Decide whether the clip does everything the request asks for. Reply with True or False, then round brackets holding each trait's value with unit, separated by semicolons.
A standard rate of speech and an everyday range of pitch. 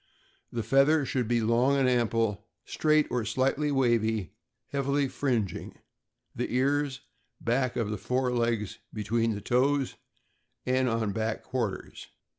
False (130 wpm; 3.1 semitones)